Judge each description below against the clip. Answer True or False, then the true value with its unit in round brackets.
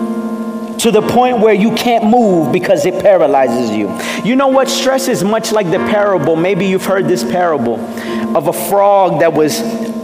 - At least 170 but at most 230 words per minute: True (180 wpm)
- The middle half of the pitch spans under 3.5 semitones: False (3.9 semitones)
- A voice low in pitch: False (215 Hz)